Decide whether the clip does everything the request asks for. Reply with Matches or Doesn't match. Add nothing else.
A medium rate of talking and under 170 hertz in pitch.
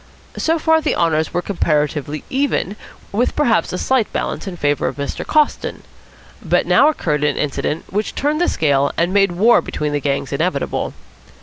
Doesn't match